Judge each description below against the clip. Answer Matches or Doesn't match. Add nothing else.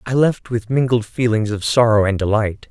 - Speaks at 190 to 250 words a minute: Matches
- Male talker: Matches